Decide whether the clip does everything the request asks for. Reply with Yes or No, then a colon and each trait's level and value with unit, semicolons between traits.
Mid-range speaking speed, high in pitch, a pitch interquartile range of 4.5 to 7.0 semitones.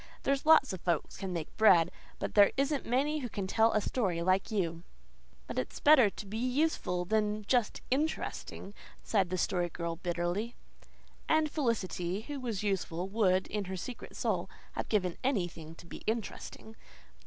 Yes: average, 165 wpm; high, 205 Hz; wide, 5.5 semitones